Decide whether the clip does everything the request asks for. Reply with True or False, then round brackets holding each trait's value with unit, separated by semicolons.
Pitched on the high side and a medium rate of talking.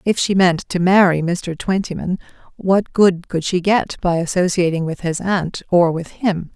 False (180 Hz; 185 wpm)